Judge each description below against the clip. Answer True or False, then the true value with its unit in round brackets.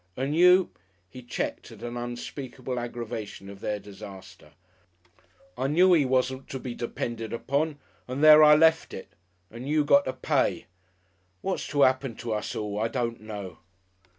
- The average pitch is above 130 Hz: False (125 Hz)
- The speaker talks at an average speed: True (165 wpm)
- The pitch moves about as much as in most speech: True (4.5 semitones)